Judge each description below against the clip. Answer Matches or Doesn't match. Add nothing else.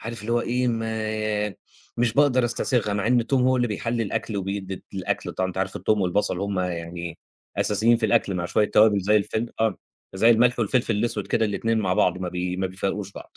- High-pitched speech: Doesn't match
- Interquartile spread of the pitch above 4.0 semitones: Doesn't match